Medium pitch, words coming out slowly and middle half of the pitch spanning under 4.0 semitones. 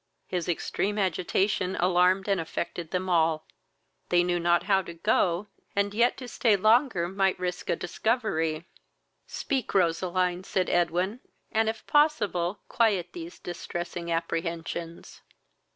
Yes: medium, 180 Hz; slow, 130 wpm; average, 2.9 semitones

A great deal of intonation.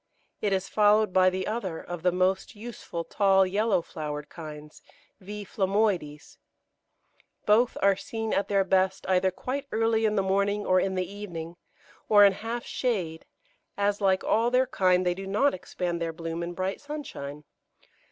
No: average, 2.9 semitones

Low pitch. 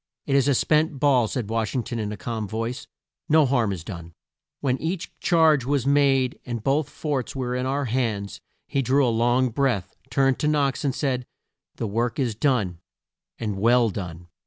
Yes: low, 125 Hz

